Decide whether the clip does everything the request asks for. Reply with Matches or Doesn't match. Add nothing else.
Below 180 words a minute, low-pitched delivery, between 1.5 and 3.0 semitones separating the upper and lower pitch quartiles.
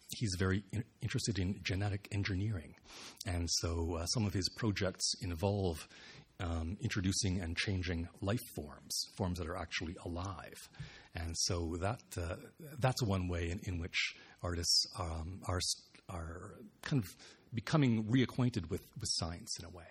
Doesn't match